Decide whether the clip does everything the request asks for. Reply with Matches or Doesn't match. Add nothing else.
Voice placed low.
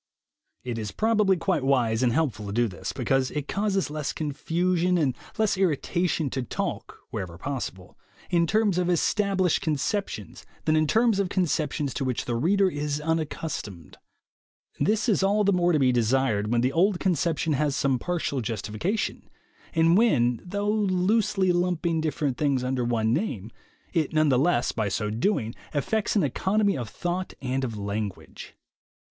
Doesn't match